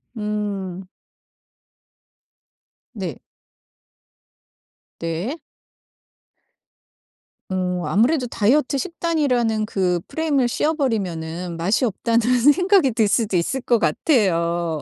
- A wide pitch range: Yes, wide, 6.8 semitones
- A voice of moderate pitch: No, high, 215 Hz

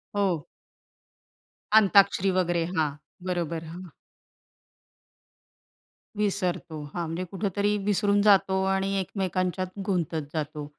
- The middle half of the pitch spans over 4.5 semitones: No, narrow, 2.6 semitones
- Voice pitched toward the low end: No, medium, 185 Hz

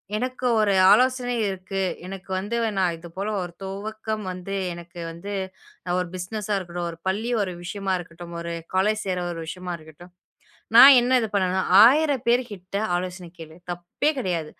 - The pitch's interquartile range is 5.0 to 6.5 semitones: No, average, 3.5 semitones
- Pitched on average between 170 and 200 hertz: Yes, high, 190 Hz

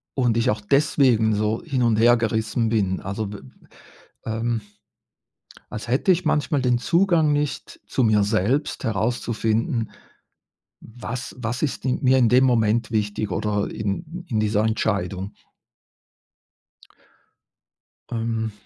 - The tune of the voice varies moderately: Yes, average, 3.0 semitones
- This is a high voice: No, low, 115 Hz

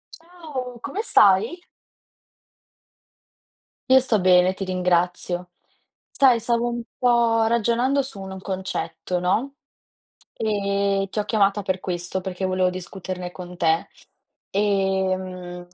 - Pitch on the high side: Yes, high, 195 Hz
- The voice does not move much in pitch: No, average, 4.3 semitones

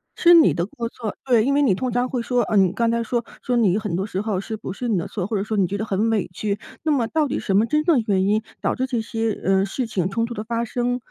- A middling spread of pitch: Yes, average, 3.5 semitones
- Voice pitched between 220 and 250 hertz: Yes, high, 225 Hz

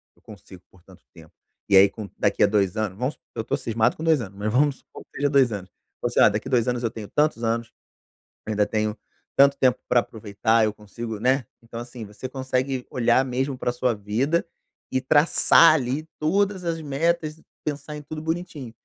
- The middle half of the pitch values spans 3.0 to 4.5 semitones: No, average, 4.9 semitones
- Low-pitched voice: Yes, low, 125 Hz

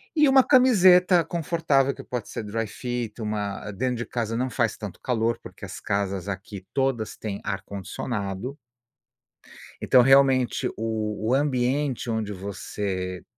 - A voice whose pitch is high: No, low, 115 Hz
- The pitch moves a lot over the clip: No, average, 4.7 semitones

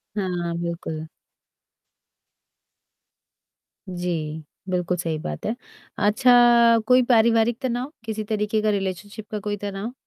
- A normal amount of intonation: Yes, average, 4.0 semitones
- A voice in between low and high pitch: No, high, 205 Hz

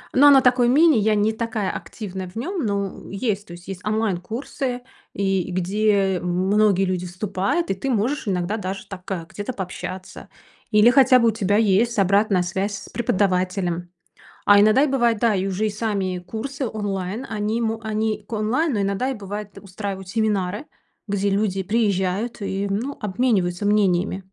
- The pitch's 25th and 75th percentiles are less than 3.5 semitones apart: Yes, average, 2.9 semitones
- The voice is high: Yes, high, 205 Hz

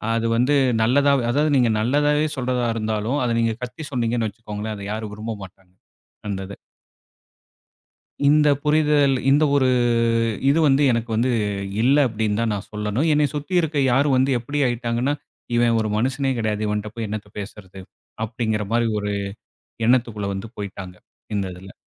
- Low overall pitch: Yes, low, 115 Hz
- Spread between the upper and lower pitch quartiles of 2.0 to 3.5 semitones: No, average, 4.5 semitones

